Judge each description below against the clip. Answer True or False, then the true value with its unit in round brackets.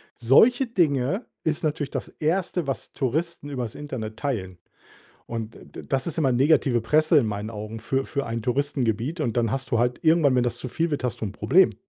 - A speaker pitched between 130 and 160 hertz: True (135 Hz)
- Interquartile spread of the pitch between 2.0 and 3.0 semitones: False (5.0 semitones)